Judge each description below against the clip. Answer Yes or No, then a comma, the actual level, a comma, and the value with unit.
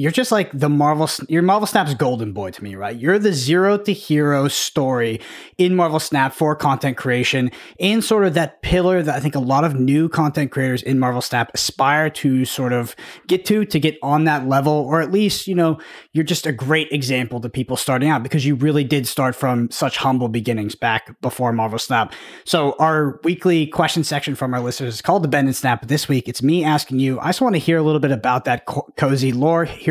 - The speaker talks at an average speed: No, fast, 230 wpm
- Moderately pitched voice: Yes, medium, 145 Hz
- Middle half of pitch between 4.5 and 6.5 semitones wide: No, average, 3.7 semitones